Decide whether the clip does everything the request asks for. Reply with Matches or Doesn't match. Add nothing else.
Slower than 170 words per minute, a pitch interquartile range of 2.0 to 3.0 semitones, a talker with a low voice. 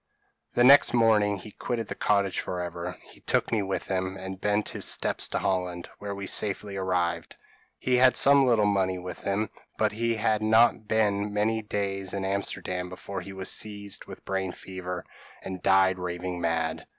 Doesn't match